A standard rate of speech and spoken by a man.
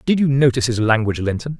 No: fast, 225 wpm; male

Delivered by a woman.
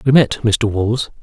No: male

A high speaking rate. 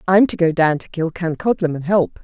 Yes: fast, 215 wpm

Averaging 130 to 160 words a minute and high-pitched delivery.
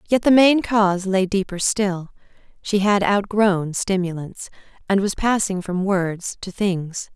Yes: average, 150 wpm; high, 195 Hz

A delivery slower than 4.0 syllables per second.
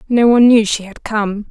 No: 5.3 syllables/s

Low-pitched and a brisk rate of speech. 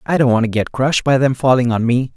Yes: low, 125 Hz; fast, 305 wpm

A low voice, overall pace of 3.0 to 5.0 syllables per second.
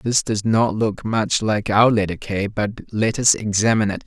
Yes: low, 110 Hz; 4.5 syllables/s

